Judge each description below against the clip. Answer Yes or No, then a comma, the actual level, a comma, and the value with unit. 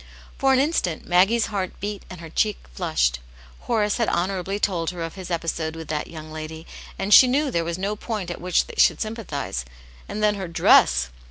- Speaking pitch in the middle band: Yes, medium, 180 Hz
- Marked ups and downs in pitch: No, average, 4.4 semitones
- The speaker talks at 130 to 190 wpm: No, average, 200 wpm